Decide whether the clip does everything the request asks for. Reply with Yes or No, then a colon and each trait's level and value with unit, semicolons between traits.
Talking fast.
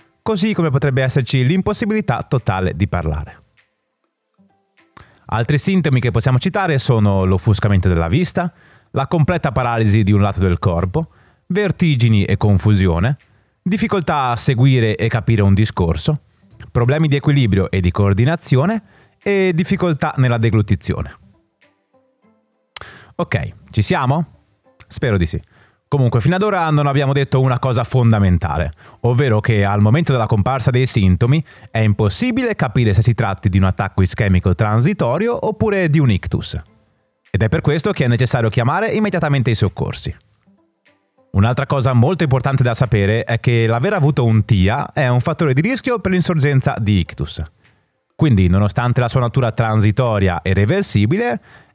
No: average, 145 wpm